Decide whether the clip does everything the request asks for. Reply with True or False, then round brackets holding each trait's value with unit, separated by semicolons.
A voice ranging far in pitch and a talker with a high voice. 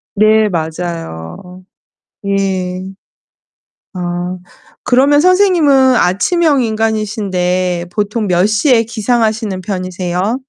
False (4.3 semitones; 200 Hz)